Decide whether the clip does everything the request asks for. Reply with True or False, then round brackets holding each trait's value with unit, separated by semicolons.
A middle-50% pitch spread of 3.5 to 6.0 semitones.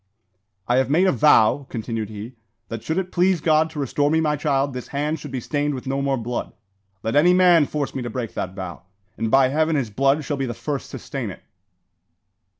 True (4.0 semitones)